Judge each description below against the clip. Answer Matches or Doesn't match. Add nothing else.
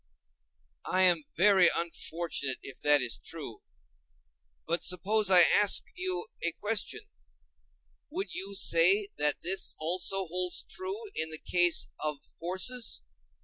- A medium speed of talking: Doesn't match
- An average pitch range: Matches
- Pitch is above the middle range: Doesn't match